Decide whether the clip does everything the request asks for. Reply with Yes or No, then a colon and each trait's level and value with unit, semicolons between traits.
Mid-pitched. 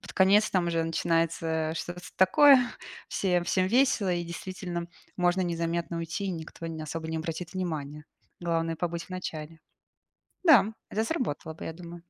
Yes: medium, 170 Hz